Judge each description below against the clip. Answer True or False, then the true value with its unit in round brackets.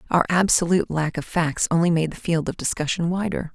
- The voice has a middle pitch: True (170 Hz)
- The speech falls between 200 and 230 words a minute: True (205 wpm)